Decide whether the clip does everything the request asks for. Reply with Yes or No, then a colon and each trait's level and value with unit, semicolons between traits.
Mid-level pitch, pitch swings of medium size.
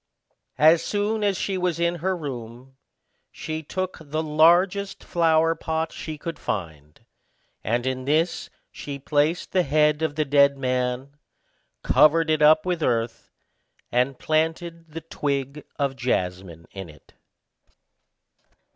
Yes: medium, 150 Hz; average, 4.1 semitones